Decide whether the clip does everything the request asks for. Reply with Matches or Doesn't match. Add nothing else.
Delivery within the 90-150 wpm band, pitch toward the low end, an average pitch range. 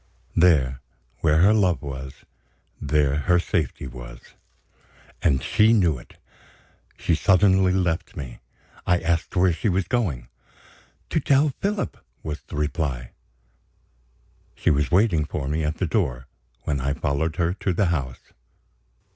Matches